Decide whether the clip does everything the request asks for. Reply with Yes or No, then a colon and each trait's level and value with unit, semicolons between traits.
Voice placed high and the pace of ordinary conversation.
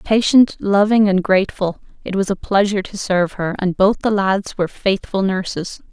Yes: high, 195 Hz; average, 180 wpm